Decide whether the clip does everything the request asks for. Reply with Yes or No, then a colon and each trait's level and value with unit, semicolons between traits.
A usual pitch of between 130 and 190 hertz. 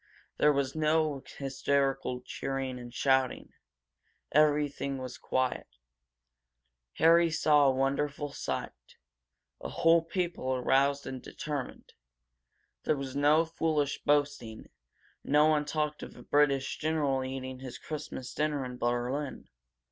Yes: medium, 140 Hz